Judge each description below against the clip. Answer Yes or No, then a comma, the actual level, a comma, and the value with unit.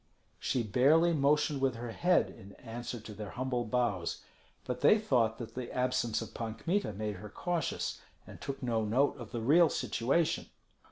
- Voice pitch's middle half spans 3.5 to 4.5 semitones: Yes, average, 4.2 semitones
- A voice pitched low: Yes, low, 125 Hz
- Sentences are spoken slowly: No, average, 175 wpm